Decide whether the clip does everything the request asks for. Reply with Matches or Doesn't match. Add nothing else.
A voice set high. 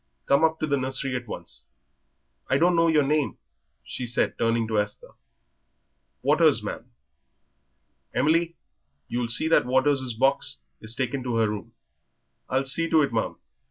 Doesn't match